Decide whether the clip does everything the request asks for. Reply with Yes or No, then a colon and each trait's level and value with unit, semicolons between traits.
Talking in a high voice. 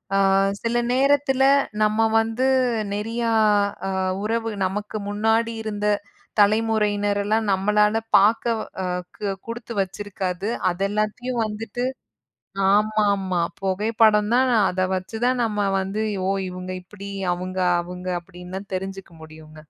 Yes: high, 210 Hz